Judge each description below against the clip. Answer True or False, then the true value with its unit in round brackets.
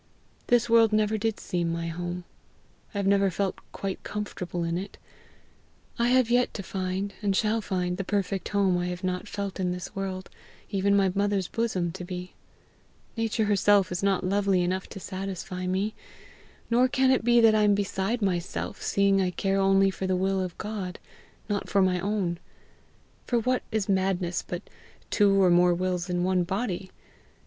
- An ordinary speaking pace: True (175 wpm)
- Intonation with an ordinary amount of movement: False (2.2 semitones)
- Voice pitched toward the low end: False (195 Hz)